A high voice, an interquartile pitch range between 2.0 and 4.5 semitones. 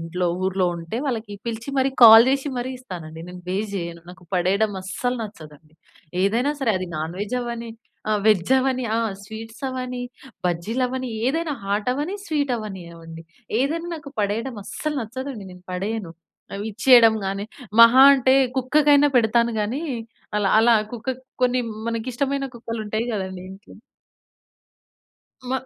No: high, 225 Hz; average, 5.0 semitones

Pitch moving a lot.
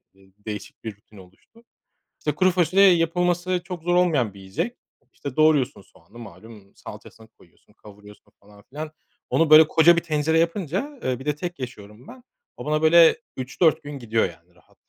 Yes: wide, 8.3 semitones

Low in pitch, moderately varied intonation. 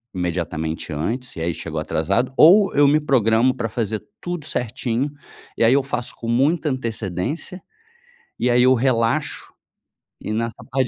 Yes: low, 120 Hz; average, 4.0 semitones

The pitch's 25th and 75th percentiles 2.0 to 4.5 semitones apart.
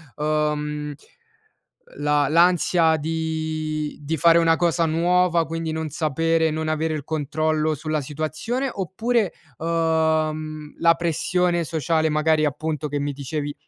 No: narrow, 1.4 semitones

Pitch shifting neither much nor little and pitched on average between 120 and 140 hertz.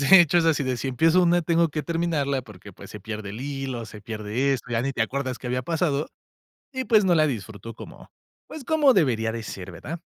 No: wide, 6.6 semitones; low, 135 Hz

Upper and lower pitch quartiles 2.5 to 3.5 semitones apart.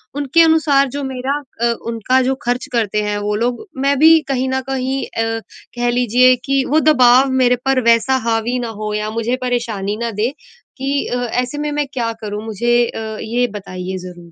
Yes: average, 3.1 semitones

